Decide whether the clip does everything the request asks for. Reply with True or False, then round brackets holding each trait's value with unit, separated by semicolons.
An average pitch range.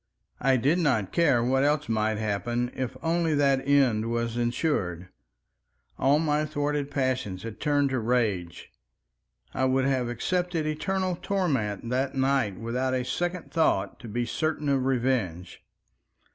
True (4.1 semitones)